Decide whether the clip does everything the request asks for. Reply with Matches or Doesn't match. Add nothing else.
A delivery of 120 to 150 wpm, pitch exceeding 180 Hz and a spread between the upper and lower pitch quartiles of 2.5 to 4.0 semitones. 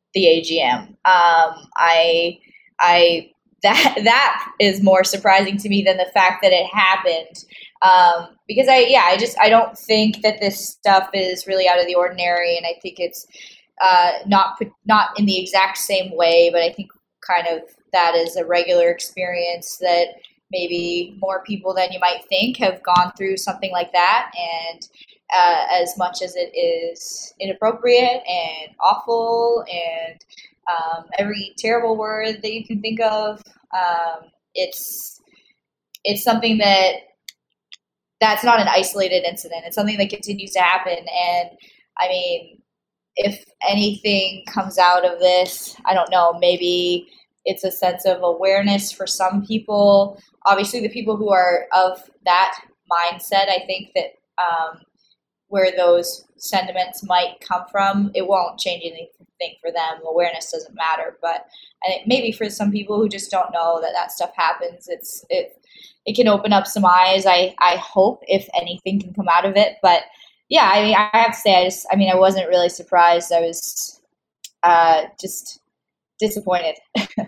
Doesn't match